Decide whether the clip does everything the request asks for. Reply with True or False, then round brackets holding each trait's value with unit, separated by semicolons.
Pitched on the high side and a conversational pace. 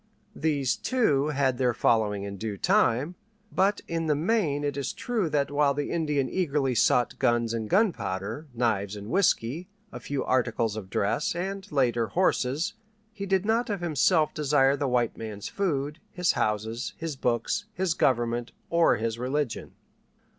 False (140 Hz; 160 wpm)